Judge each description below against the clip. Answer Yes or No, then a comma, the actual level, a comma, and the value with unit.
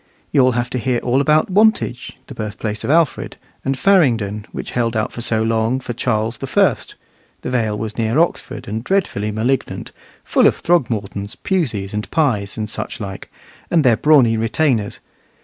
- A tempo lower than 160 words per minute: No, average, 165 wpm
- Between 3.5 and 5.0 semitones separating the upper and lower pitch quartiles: Yes, average, 4.1 semitones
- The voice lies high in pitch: No, low, 115 Hz